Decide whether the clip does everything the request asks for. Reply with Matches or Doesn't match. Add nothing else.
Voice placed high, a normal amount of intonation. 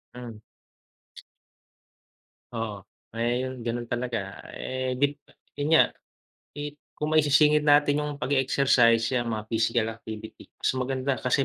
Doesn't match